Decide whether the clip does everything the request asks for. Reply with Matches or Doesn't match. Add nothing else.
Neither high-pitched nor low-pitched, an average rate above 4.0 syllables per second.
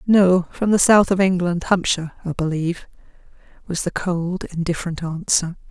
Matches